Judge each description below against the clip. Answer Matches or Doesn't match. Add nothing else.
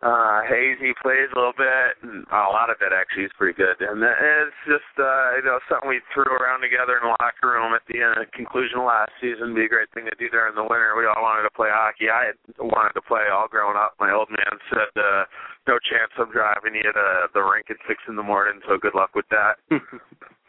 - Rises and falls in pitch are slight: Doesn't match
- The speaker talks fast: Matches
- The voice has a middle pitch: Doesn't match